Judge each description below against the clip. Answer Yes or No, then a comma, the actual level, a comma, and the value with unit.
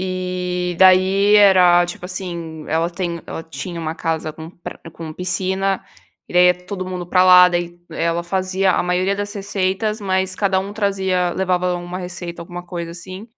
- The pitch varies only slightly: Yes, narrow, 1.5 semitones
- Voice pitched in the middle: Yes, medium, 180 Hz